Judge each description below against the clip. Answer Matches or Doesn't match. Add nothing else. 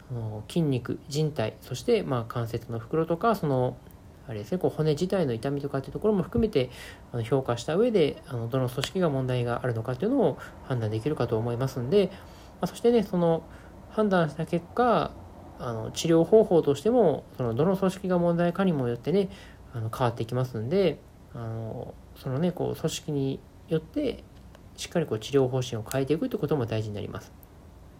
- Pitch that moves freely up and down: Matches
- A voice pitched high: Doesn't match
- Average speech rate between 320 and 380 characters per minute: Matches